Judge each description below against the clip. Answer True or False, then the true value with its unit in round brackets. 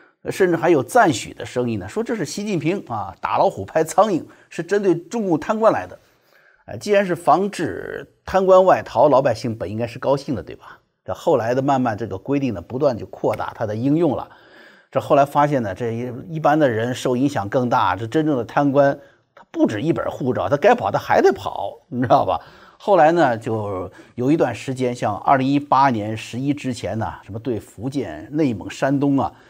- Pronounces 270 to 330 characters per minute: True (295 characters per minute)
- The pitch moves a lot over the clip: True (6.4 semitones)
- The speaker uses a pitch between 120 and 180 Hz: True (140 Hz)